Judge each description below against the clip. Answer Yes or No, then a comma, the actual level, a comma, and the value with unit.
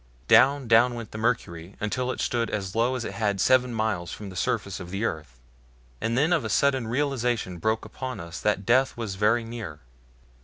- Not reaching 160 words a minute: No, fast, 205 wpm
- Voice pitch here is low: Yes, low, 115 Hz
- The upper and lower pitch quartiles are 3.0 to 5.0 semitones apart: Yes, average, 4.0 semitones